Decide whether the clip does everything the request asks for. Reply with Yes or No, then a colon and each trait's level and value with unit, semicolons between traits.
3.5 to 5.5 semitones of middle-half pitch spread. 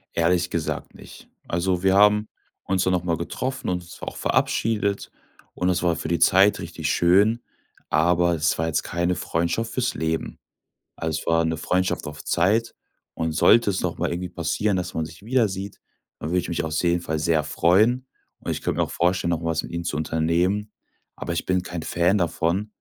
No: average, 3.0 semitones